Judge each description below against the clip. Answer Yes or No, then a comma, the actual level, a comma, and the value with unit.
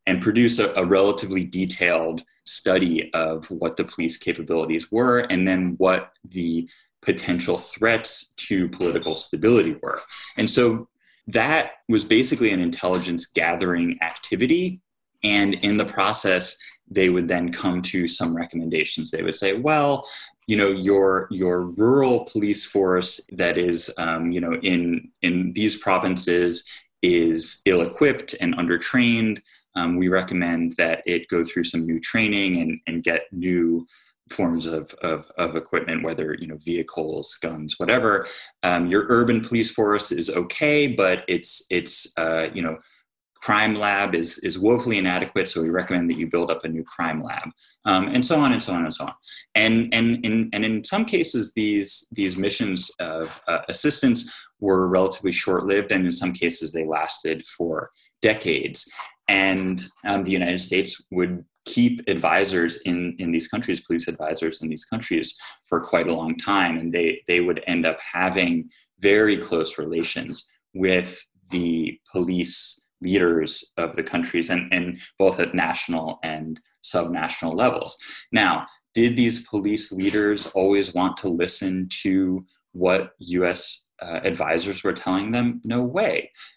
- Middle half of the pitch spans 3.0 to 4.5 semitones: Yes, average, 3.5 semitones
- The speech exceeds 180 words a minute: No, average, 155 wpm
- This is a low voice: Yes, very low, 90 Hz